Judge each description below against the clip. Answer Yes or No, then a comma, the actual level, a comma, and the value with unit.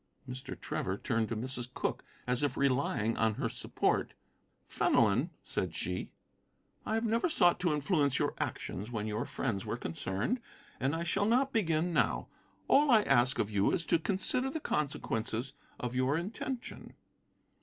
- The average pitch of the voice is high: No, low, 135 Hz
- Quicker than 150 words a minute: Yes, average, 160 wpm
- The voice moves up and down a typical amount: No, wide, 8.2 semitones